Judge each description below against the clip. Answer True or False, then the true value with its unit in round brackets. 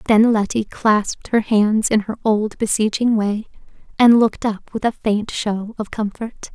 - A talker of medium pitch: False (215 Hz)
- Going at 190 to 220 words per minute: False (175 wpm)